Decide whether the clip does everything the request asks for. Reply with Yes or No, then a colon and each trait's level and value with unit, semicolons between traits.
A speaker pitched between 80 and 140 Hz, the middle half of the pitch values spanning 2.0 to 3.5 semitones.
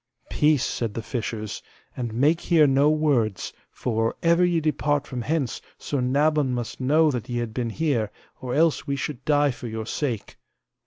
No: low, 135 Hz; average, 4.3 semitones